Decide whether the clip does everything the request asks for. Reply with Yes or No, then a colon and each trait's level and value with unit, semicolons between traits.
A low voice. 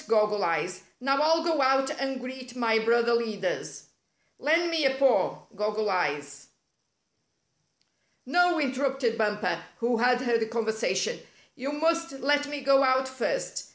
No: very high, 255 Hz